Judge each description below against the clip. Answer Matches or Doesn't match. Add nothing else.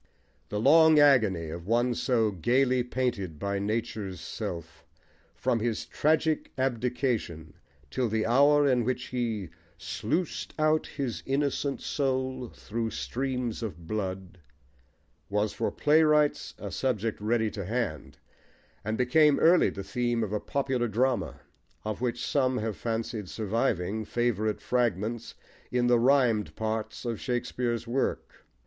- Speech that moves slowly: Matches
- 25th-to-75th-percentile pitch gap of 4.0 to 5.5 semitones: Doesn't match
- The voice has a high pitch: Doesn't match